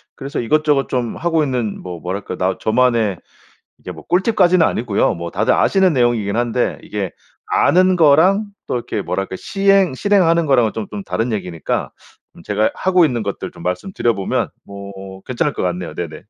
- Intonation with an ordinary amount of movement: No, wide, 8.6 semitones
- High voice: No, low, 120 Hz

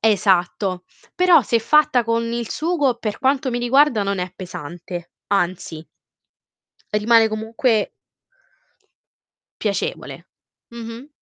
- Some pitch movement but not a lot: Yes, average, 4.9 semitones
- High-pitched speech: Yes, high, 225 Hz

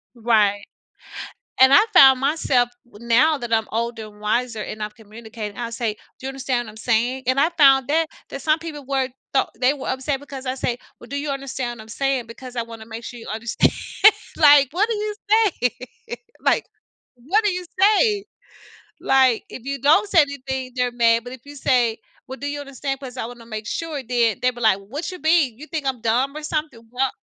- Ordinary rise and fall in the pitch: Yes, average, 3.6 semitones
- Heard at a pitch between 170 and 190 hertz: No, very high, 260 Hz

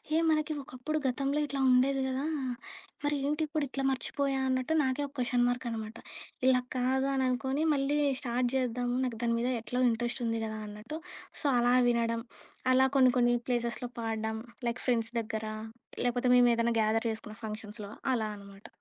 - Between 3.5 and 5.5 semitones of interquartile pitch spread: No, narrow, 2.6 semitones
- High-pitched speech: Yes, high, 245 Hz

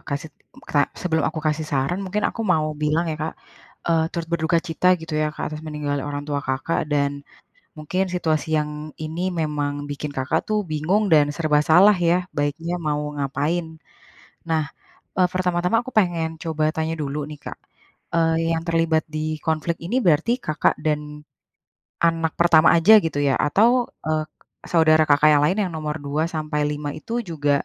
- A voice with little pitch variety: Yes, narrow, 2.0 semitones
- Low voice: No, medium, 155 Hz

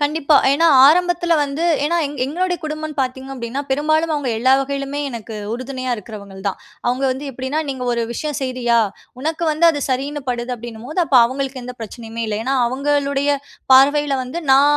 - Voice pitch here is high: Yes, very high, 275 Hz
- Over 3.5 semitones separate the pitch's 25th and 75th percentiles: No, average, 2.9 semitones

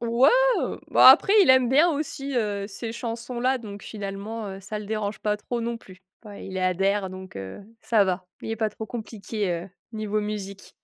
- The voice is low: No, high, 215 Hz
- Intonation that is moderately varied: Yes, average, 3.1 semitones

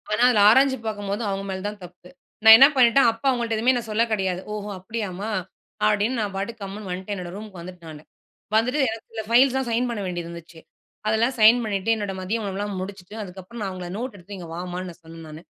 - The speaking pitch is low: No, high, 205 Hz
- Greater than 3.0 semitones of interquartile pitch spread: Yes, average, 3.5 semitones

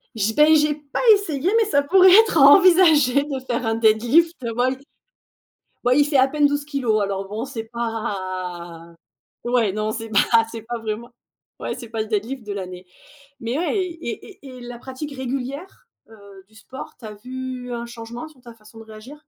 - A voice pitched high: Yes, high, 245 Hz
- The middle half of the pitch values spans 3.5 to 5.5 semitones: Yes, average, 4.6 semitones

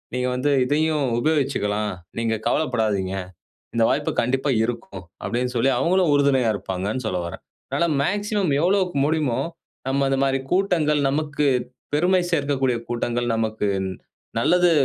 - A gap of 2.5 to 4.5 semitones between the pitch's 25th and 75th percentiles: No, average, 5.1 semitones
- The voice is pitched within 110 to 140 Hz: Yes, low, 135 Hz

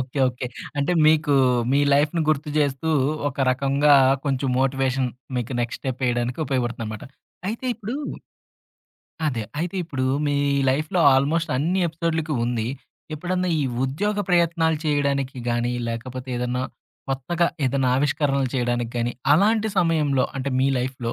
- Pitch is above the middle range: No, medium, 140 Hz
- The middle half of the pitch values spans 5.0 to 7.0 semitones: No, average, 4.1 semitones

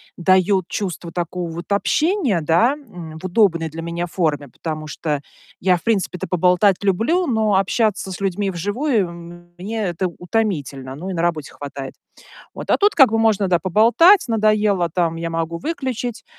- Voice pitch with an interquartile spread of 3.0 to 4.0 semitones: No, average, 4.6 semitones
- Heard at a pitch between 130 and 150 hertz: No, medium, 185 Hz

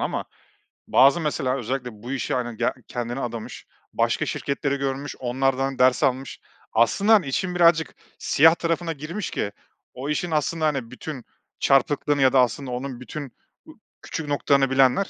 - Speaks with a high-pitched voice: No, low, 135 Hz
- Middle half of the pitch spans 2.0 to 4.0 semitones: Yes, average, 3.2 semitones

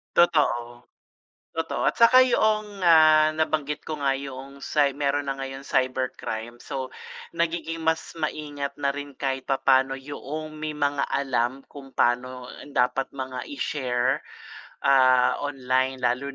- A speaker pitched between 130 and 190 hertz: Yes, medium, 140 Hz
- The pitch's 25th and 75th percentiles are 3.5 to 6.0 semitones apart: No, average, 2.9 semitones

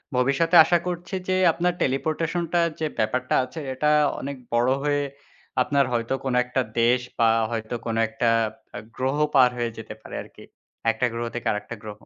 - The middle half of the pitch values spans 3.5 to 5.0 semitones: Yes, average, 4.2 semitones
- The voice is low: Yes, low, 130 Hz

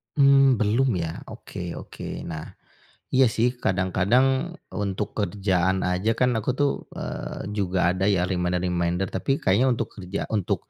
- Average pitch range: Yes, average, 3.7 semitones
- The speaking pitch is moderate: No, very low, 95 Hz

